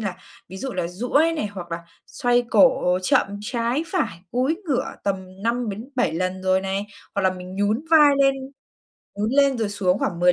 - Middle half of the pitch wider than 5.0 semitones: Yes, wide, 5.5 semitones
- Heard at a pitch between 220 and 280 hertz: No, high, 210 Hz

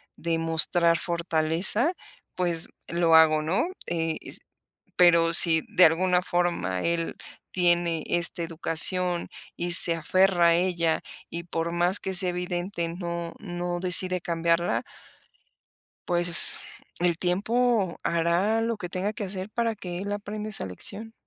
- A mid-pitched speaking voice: Yes, medium, 175 Hz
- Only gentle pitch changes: Yes, narrow, 1.7 semitones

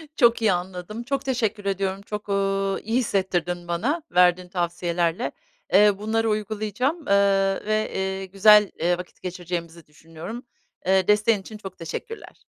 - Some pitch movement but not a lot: Yes, average, 3.2 semitones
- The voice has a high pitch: Yes, high, 195 Hz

